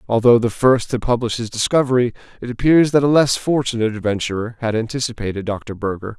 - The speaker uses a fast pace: No, average, 175 wpm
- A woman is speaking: No, male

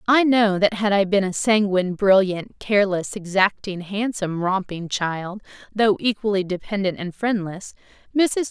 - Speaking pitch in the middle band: No, high, 200 Hz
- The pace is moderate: No, slow, 125 wpm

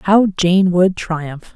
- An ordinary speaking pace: Yes, average, 155 wpm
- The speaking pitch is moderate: Yes, medium, 180 Hz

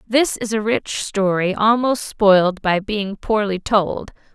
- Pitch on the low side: No, high, 210 Hz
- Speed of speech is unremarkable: Yes, average, 150 wpm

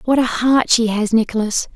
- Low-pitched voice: No, high, 230 Hz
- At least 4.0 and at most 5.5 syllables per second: Yes, 5.0 syllables/s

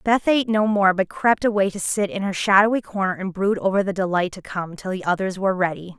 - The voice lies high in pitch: Yes, high, 195 Hz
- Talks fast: Yes, fast, 250 wpm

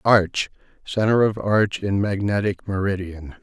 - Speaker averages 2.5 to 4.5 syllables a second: Yes, 4.1 syllables/s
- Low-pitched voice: Yes, low, 100 Hz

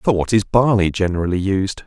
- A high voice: No, low, 100 Hz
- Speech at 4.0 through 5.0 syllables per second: No, 5.5 syllables/s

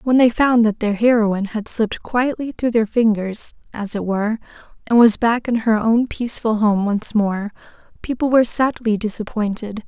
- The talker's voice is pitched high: Yes, high, 225 Hz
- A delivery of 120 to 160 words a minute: No, average, 175 wpm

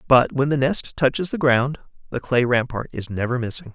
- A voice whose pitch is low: Yes, low, 130 Hz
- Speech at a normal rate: No, fast, 210 wpm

